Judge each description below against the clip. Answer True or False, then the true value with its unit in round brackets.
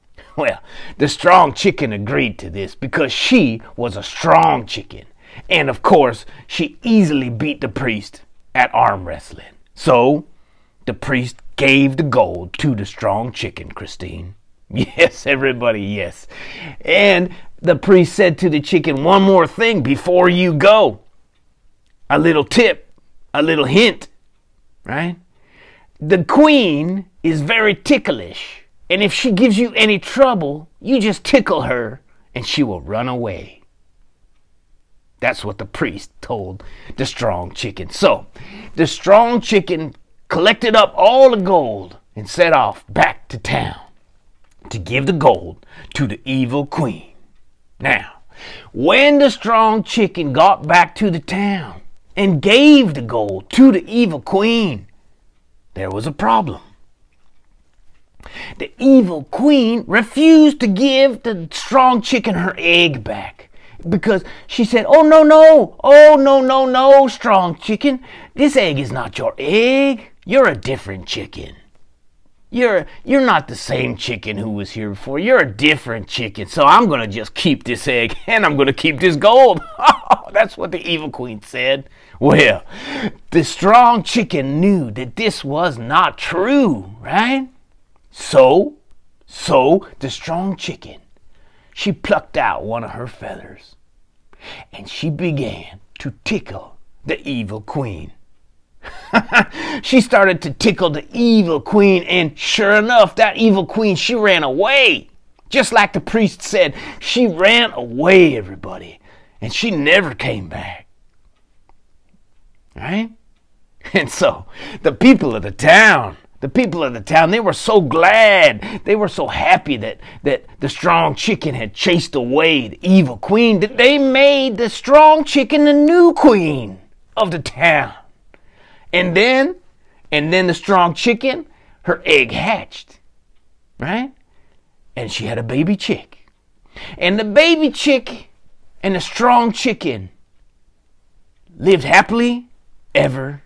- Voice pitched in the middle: True (180 Hz)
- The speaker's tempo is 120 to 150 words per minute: True (140 wpm)